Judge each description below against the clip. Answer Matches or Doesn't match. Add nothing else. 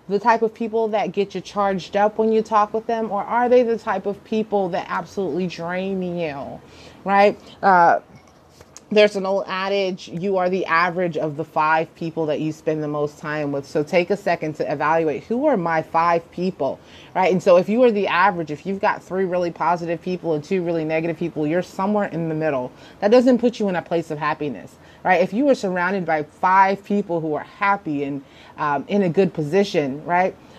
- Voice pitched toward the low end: Doesn't match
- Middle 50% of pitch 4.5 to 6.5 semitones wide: Doesn't match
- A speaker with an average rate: Doesn't match